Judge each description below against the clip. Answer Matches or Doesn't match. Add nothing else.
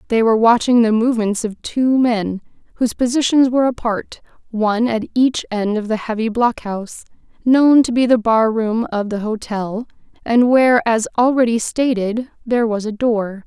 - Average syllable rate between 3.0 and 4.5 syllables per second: Doesn't match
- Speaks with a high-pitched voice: Matches